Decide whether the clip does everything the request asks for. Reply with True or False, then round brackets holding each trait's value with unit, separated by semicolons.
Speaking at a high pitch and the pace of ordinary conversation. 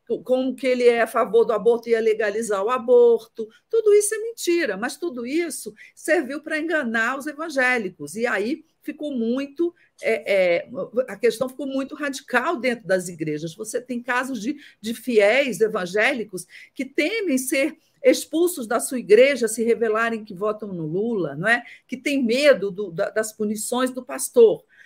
True (245 Hz; 155 wpm)